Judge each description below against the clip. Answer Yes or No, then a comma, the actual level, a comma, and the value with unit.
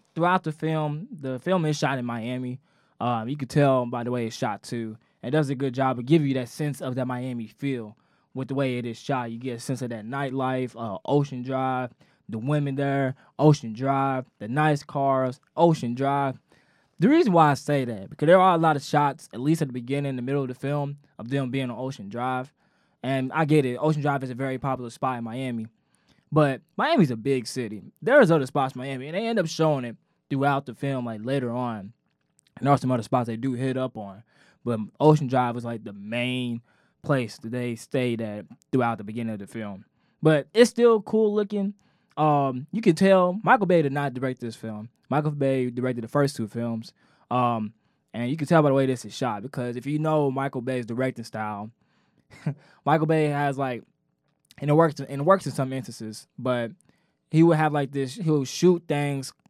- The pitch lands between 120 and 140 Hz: Yes, low, 135 Hz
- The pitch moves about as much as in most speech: Yes, average, 3.7 semitones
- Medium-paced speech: No, fast, 220 wpm